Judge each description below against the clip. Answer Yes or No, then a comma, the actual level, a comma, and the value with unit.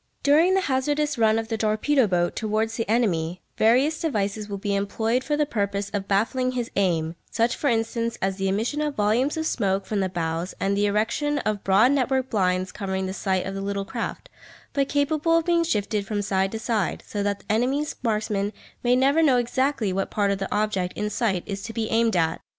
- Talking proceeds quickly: Yes, fast, 210 wpm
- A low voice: No, high, 215 Hz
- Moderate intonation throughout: Yes, average, 4.6 semitones